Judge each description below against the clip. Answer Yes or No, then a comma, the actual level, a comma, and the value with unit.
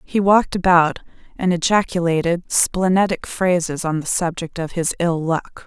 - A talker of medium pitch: Yes, medium, 175 Hz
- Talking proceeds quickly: No, average, 150 wpm